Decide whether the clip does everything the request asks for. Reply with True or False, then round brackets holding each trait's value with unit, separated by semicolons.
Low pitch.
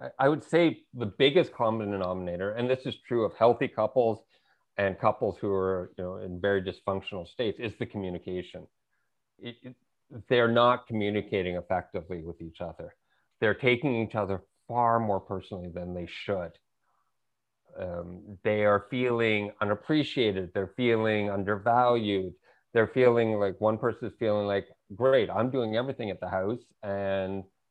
True (105 Hz)